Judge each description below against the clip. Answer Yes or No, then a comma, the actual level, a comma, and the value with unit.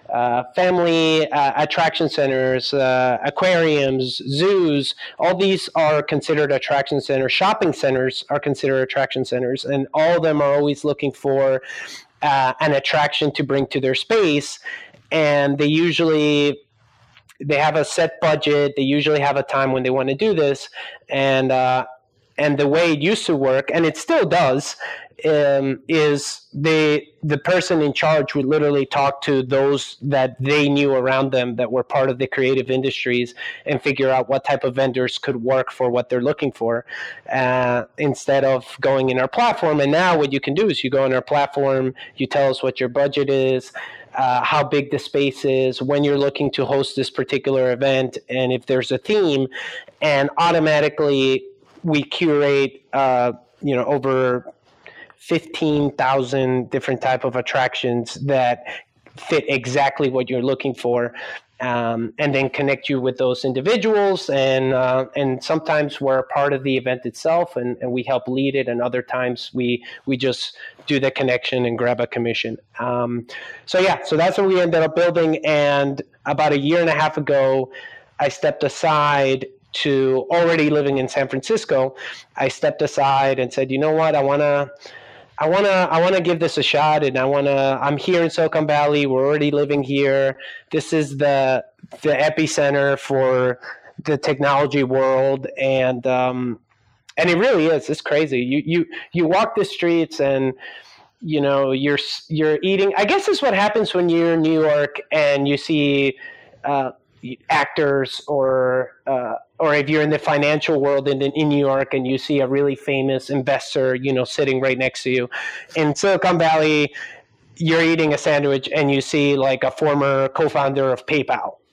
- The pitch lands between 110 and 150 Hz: Yes, medium, 140 Hz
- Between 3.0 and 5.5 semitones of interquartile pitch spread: No, narrow, 2.5 semitones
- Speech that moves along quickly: No, average, 175 wpm